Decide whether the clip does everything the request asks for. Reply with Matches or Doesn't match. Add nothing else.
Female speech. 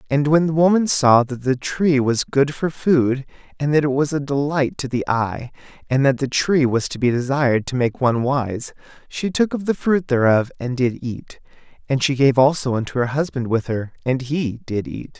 Doesn't match